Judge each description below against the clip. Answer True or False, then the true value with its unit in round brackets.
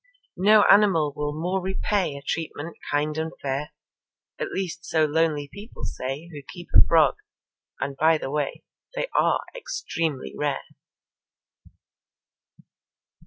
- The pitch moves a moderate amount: True (3.9 semitones)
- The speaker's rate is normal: False (125 wpm)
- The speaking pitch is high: False (160 Hz)